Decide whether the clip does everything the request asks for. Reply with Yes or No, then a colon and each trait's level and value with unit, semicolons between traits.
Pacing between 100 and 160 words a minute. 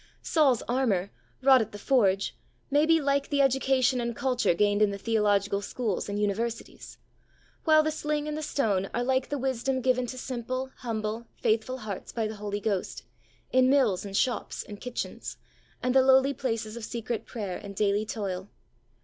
No: average, 175 wpm